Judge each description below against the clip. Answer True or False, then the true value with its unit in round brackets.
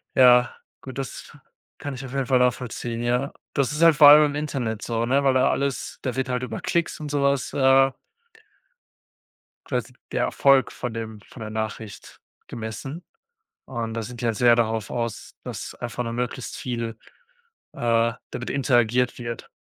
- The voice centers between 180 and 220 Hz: False (125 Hz)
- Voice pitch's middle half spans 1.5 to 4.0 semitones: True (2.7 semitones)